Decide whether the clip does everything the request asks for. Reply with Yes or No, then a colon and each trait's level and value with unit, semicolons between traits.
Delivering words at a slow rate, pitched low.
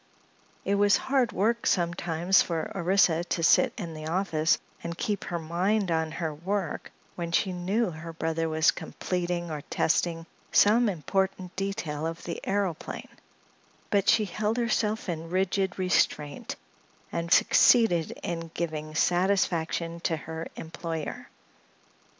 No: slow, 130 wpm; medium, 175 Hz